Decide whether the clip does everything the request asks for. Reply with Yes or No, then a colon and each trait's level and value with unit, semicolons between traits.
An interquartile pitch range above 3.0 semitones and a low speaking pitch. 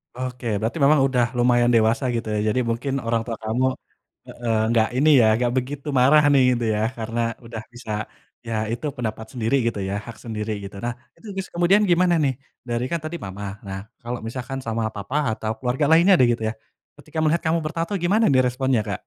Yes: average, 3.7 semitones; low, 120 Hz